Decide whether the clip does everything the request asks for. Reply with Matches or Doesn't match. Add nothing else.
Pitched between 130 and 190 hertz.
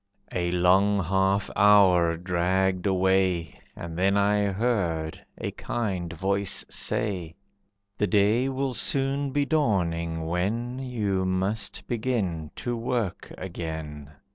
Doesn't match